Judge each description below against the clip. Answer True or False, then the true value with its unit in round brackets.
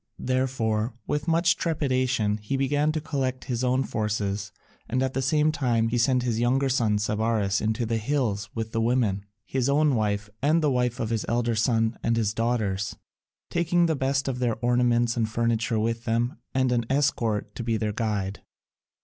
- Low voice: True (120 Hz)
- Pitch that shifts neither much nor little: True (3.3 semitones)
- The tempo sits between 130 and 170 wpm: False (185 wpm)